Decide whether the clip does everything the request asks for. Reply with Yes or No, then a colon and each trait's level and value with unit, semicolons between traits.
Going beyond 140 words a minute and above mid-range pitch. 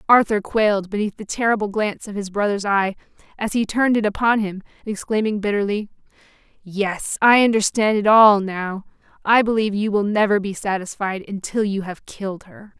Yes: average, 170 wpm; high, 205 Hz